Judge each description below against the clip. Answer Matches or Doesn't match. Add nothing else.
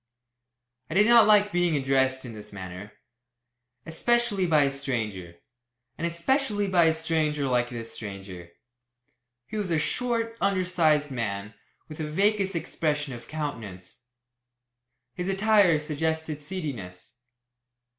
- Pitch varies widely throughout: Matches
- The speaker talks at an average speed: Doesn't match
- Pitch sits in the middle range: Matches